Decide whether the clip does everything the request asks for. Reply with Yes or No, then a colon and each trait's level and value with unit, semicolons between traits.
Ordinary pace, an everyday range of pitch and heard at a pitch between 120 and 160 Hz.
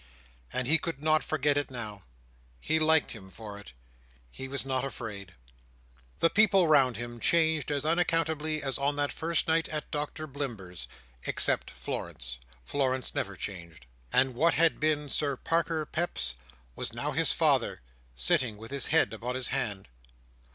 No: average, 150 wpm; wide, 6.3 semitones; medium, 140 Hz